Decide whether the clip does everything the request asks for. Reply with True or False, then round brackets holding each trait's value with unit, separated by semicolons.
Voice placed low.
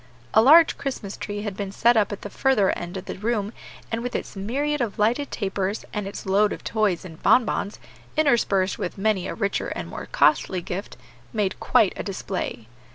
False (205 Hz)